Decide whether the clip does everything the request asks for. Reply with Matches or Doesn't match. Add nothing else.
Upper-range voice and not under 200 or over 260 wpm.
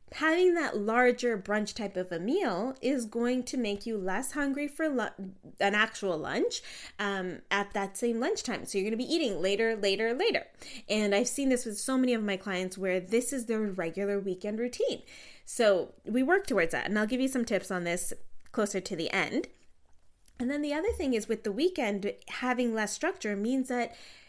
Matches